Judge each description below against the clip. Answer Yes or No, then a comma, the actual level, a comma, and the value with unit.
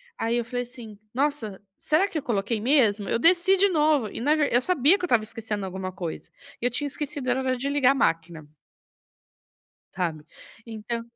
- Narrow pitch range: No, wide, 5.6 semitones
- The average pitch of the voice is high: Yes, high, 245 Hz